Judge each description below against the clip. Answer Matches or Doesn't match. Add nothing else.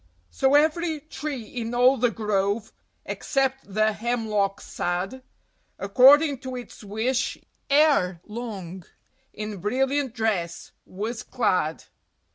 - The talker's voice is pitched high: Matches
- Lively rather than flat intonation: Doesn't match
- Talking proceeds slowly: Matches